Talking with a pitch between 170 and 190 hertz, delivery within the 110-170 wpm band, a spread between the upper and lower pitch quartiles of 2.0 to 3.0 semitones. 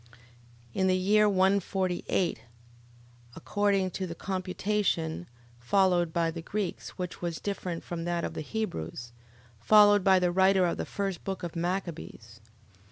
Yes: medium, 185 Hz; average, 145 wpm; narrow, 2.6 semitones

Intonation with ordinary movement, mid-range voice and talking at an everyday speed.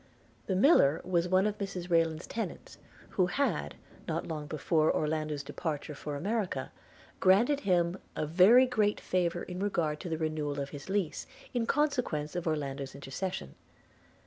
Yes: average, 4.6 semitones; medium, 170 Hz; average, 150 wpm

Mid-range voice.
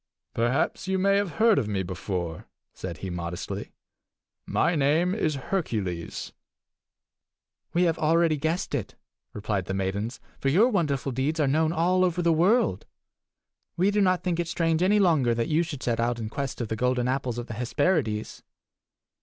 Yes: medium, 145 Hz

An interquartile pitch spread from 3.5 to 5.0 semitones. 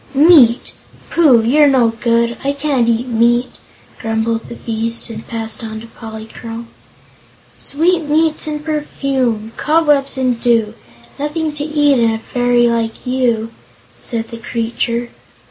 Yes: average, 4.0 semitones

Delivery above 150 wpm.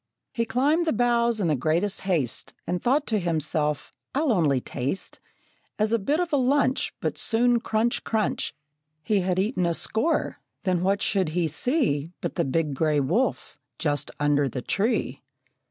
Yes: average, 170 wpm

